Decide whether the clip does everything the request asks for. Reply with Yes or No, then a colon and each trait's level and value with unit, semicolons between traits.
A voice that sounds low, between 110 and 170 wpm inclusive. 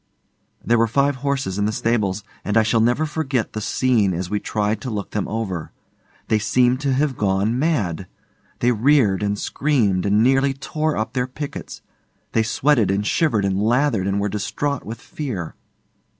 No: low, 115 Hz; average, 180 wpm